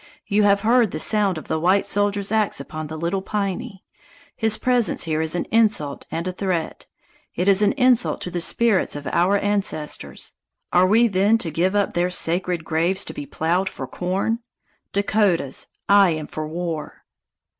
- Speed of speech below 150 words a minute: No, average, 175 wpm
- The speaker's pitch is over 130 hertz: Yes, high, 190 Hz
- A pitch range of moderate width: Yes, average, 3.6 semitones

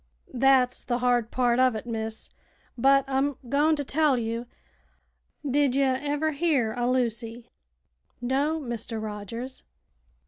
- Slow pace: Yes, slow, 130 wpm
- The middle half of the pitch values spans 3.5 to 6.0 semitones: No, average, 2.8 semitones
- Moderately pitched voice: No, very high, 255 Hz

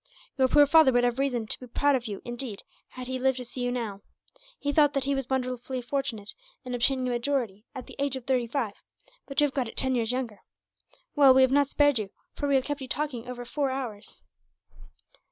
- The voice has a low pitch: No, very high, 255 Hz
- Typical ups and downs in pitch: No, narrow, 2.3 semitones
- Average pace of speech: No, fast, 230 wpm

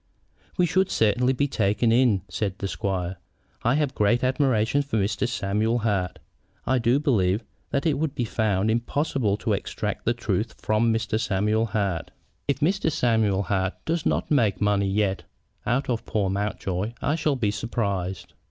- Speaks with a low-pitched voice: Yes, low, 110 Hz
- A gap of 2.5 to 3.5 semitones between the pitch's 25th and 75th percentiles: No, average, 4.6 semitones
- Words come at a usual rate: Yes, average, 165 wpm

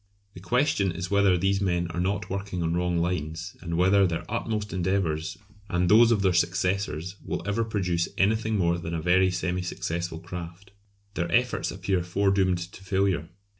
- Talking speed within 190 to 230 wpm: No, average, 170 wpm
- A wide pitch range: No, narrow, 2.4 semitones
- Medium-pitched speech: No, very low, 90 Hz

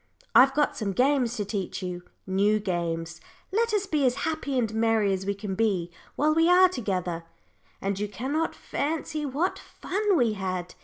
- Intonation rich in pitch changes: Yes, wide, 7.6 semitones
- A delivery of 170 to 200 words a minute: Yes, average, 175 wpm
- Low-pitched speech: No, high, 225 Hz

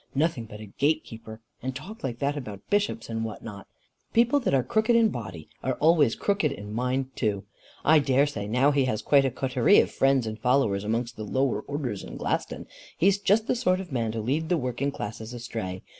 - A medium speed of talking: No, fast, 215 wpm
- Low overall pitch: Yes, low, 130 Hz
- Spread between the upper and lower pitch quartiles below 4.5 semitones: No, average, 5.1 semitones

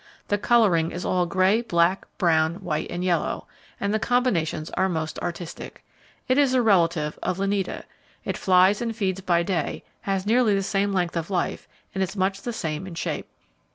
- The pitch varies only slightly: No, average, 3.1 semitones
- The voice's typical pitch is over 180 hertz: Yes, high, 190 Hz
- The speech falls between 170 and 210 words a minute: Yes, average, 185 wpm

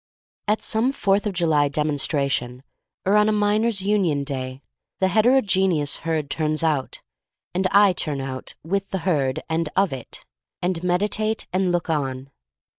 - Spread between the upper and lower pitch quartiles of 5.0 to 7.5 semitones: Yes, wide, 5.5 semitones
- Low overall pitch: No, medium, 175 Hz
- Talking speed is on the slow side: No, average, 160 wpm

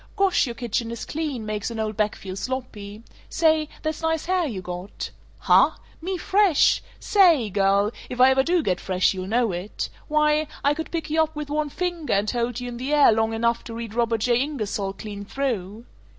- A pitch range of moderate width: No, wide, 6.3 semitones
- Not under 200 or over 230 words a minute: Yes, fast, 205 wpm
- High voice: Yes, high, 240 Hz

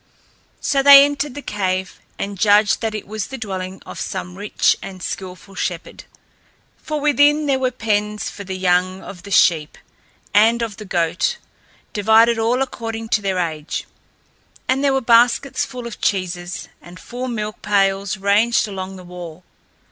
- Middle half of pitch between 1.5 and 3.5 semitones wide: No, average, 4.1 semitones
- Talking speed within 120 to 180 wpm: Yes, average, 165 wpm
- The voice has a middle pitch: No, high, 205 Hz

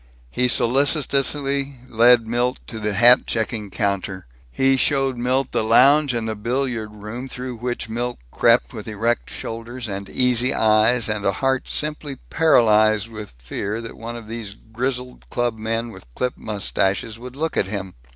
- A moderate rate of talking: Yes, average, 160 wpm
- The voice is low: Yes, low, 115 Hz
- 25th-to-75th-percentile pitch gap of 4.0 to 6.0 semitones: No, average, 2.8 semitones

